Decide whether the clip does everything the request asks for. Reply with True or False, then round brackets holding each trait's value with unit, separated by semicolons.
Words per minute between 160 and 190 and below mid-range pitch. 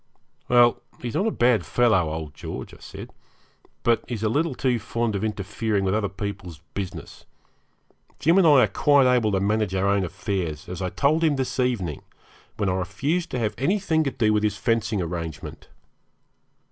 True (185 wpm; 110 Hz)